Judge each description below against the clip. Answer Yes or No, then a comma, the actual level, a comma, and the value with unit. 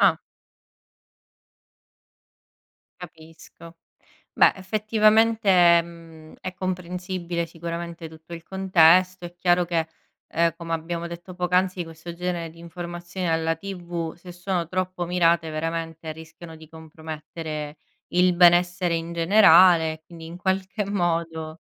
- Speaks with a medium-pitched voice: Yes, medium, 170 Hz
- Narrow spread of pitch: Yes, narrow, 1.7 semitones